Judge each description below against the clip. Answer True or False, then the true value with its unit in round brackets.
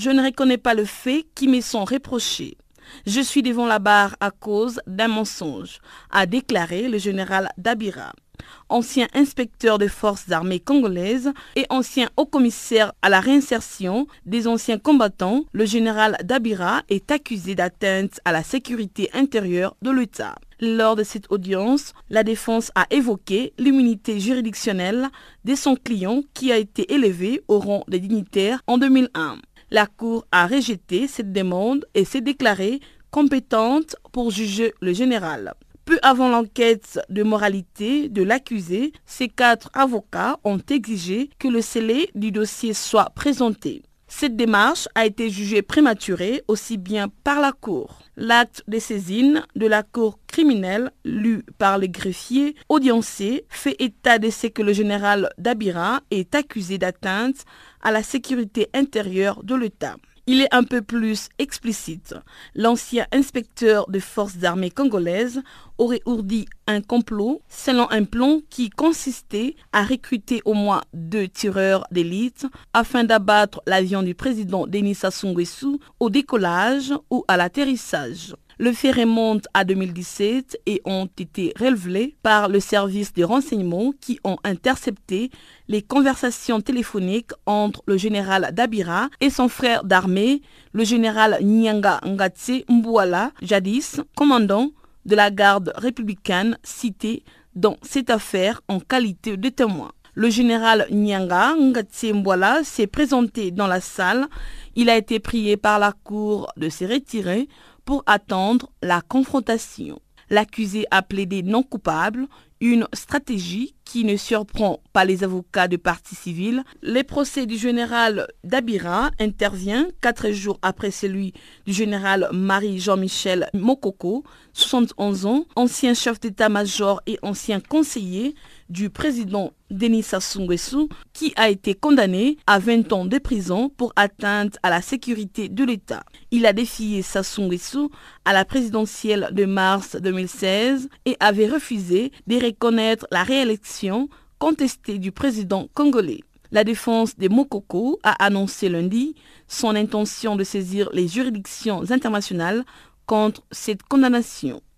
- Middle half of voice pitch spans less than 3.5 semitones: False (4.1 semitones)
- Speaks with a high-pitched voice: True (225 Hz)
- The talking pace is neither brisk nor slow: False (135 wpm)